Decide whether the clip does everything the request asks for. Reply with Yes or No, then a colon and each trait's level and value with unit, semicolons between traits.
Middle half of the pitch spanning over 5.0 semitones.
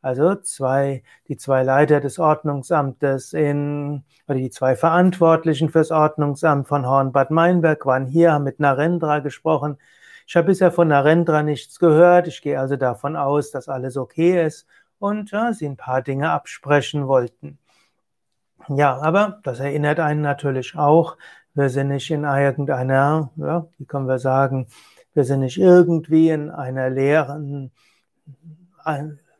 No: average, 2.8 semitones